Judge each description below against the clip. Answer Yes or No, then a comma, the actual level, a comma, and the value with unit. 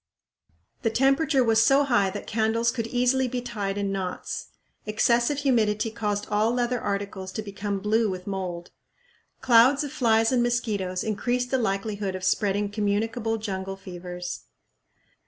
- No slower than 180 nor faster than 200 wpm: No, average, 145 wpm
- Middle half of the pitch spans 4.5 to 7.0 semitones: No, average, 3.4 semitones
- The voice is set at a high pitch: Yes, high, 220 Hz